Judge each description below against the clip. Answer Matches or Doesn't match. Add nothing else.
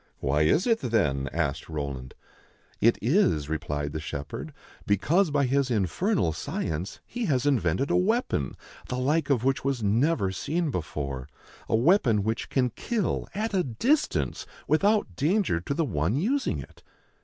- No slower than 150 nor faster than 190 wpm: Matches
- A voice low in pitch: Matches